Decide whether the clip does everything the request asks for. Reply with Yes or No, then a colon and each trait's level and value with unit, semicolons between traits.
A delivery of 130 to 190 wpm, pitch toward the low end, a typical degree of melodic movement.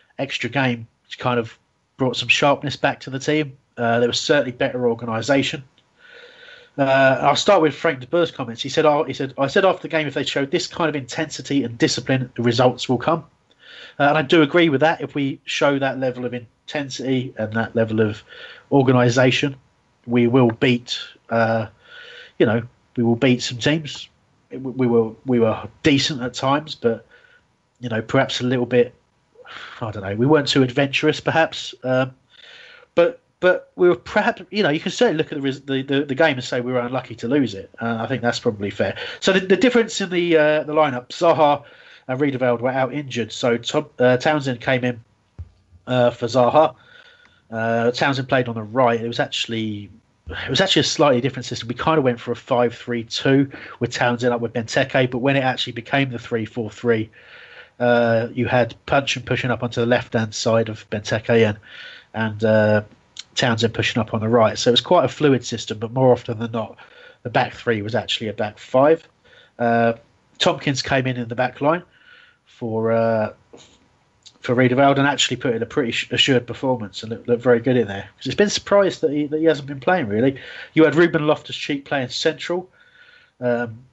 No: average, 200 wpm; low, 130 Hz; average, 3.8 semitones